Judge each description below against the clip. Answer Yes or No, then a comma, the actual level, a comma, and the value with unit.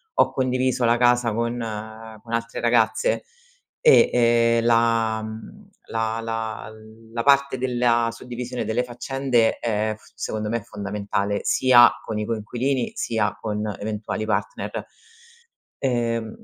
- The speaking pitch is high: No, low, 115 Hz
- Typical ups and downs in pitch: No, narrow, 1.9 semitones